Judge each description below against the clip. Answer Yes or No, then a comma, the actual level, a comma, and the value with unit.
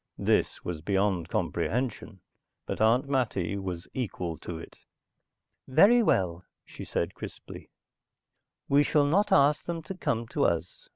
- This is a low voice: Yes, low, 110 Hz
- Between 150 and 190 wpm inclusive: No, slow, 135 wpm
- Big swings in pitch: Yes, wide, 8.0 semitones